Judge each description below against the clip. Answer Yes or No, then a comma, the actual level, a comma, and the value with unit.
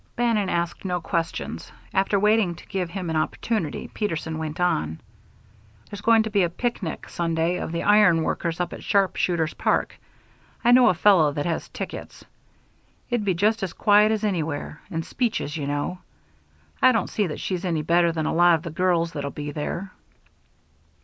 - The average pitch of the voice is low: No, medium, 175 Hz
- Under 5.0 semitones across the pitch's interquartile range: Yes, average, 4.1 semitones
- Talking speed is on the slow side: No, average, 180 wpm